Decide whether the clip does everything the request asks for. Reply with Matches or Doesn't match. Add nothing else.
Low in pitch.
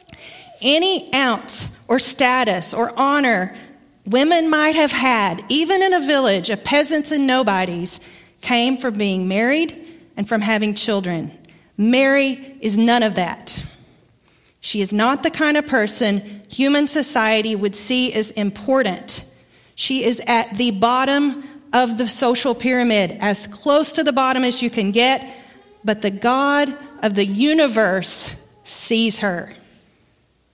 Doesn't match